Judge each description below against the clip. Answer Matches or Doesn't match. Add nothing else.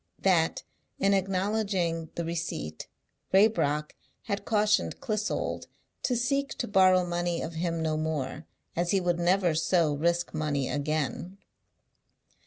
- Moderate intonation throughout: Matches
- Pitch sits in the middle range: Matches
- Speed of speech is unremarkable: Doesn't match